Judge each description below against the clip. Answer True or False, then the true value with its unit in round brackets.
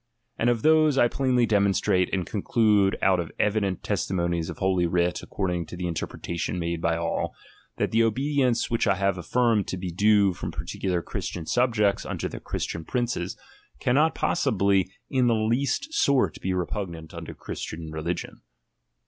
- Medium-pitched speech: False (100 Hz)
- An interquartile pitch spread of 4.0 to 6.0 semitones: True (5.2 semitones)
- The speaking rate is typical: True (160 wpm)